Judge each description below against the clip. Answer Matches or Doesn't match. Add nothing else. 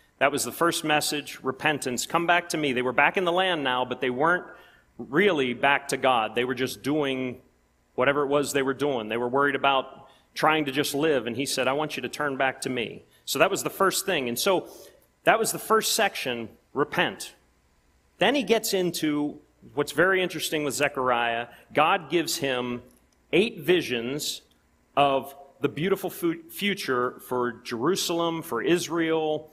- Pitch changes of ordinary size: Matches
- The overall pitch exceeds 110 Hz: Matches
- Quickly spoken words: Doesn't match